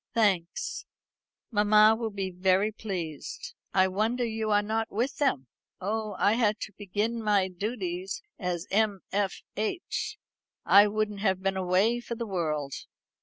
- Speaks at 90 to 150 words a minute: Yes, average, 145 wpm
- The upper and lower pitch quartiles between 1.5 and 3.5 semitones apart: Yes, average, 2.8 semitones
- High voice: Yes, high, 205 Hz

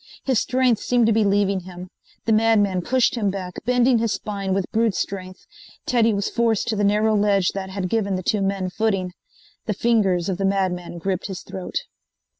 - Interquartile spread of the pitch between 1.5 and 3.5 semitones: Yes, average, 3.0 semitones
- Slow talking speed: No, average, 195 wpm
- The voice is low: No, high, 200 Hz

